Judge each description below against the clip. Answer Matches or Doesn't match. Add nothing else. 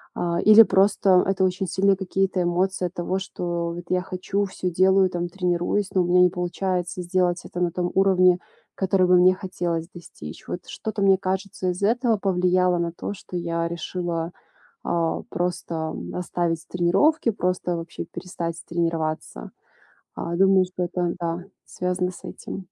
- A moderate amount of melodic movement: Doesn't match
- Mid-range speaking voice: Matches